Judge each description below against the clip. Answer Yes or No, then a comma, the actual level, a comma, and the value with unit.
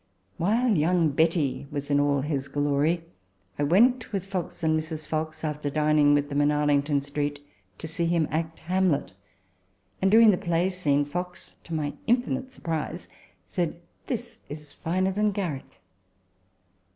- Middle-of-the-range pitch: Yes, medium, 155 Hz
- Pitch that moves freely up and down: No, average, 3.7 semitones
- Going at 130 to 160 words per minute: Yes, average, 155 wpm